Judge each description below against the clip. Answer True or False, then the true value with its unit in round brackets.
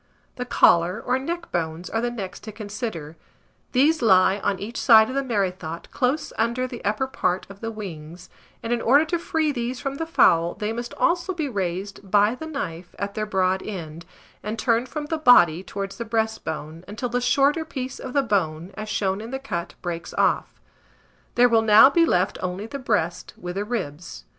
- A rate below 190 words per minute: False (195 wpm)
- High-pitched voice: True (215 Hz)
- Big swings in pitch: True (5.7 semitones)